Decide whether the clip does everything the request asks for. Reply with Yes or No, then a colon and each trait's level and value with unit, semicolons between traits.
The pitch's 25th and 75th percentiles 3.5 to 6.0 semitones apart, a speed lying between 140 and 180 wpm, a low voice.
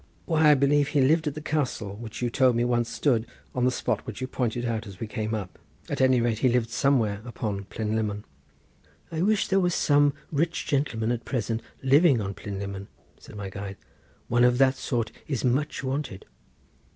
No: average, 4.4 semitones; average, 200 wpm; low, 120 Hz